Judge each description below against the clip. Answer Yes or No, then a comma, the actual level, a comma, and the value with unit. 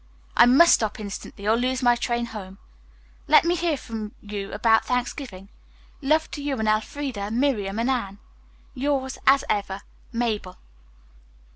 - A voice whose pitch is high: Yes, high, 235 Hz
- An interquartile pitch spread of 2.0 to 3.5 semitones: No, average, 4.3 semitones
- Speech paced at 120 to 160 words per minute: Yes, average, 145 wpm